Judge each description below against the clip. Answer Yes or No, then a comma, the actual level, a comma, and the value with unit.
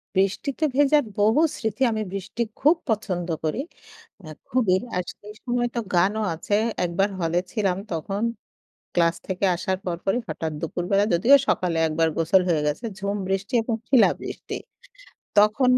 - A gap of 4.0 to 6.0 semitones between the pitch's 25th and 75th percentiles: Yes, average, 4.4 semitones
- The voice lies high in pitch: Yes, high, 195 Hz